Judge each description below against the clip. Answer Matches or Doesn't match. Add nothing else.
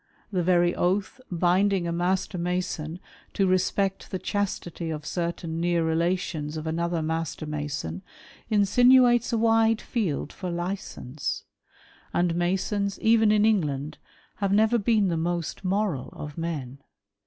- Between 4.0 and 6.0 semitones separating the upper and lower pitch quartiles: Doesn't match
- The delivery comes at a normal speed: Doesn't match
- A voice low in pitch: Doesn't match